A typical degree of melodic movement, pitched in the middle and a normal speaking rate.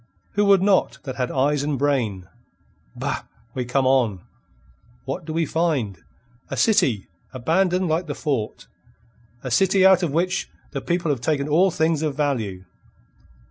Yes: average, 5.0 semitones; medium, 150 Hz; average, 155 wpm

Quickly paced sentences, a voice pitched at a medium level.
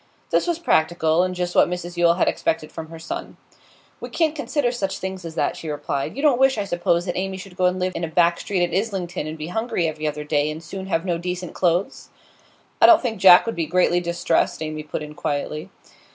Yes: fast, 235 wpm; medium, 175 Hz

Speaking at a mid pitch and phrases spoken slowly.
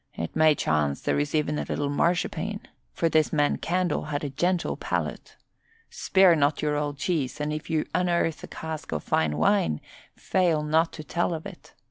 No: medium, 155 Hz; average, 185 wpm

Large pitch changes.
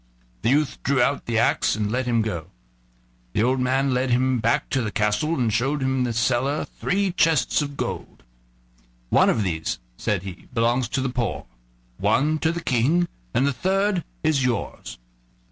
No: average, 3.7 semitones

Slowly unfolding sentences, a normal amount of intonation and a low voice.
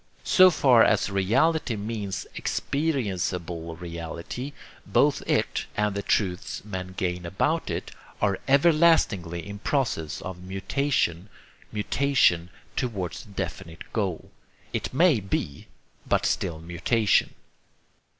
No: slow, 110 wpm; wide, 6.7 semitones; low, 100 Hz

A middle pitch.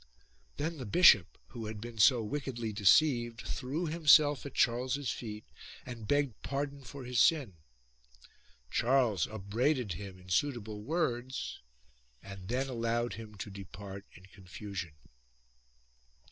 No: low, 120 Hz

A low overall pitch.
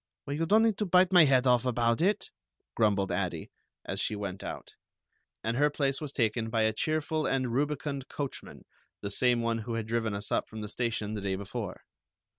Yes: low, 120 Hz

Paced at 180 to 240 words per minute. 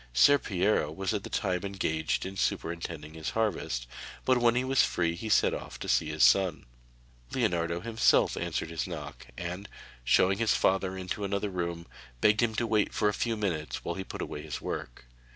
Yes: average, 190 wpm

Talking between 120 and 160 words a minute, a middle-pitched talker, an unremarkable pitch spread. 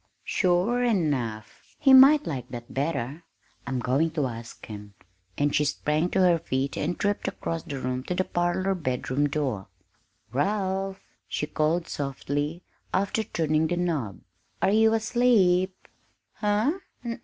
No: average, 140 wpm; medium, 165 Hz; wide, 5.9 semitones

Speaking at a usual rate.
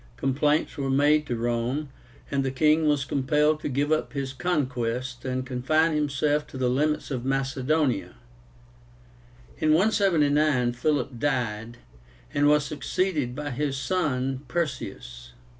No: slow, 130 wpm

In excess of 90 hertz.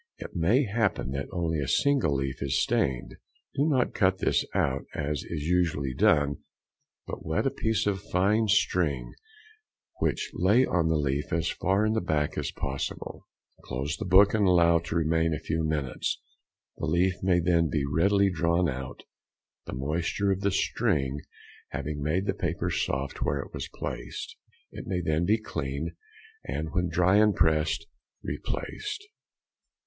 No: very low, 85 Hz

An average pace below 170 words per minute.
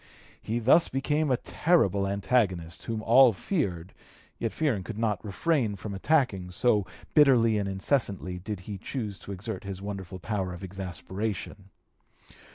Yes: average, 145 wpm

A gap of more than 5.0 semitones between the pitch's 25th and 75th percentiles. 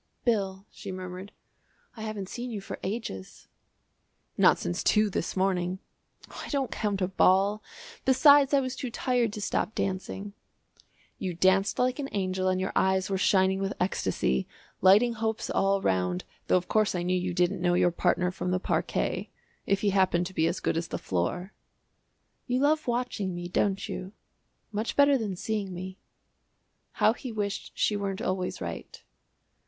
No: average, 3.0 semitones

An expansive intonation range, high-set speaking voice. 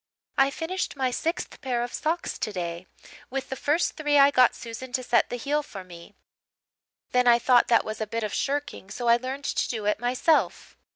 No: average, 3.8 semitones; very high, 250 Hz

